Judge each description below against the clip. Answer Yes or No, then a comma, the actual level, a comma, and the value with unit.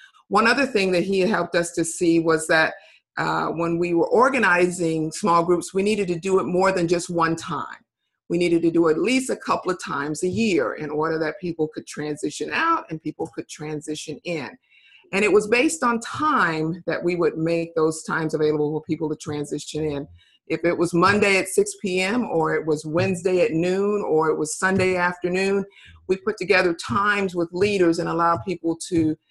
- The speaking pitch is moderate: Yes, medium, 170 Hz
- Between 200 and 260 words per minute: Yes, fast, 205 wpm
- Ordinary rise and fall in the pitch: Yes, average, 3.0 semitones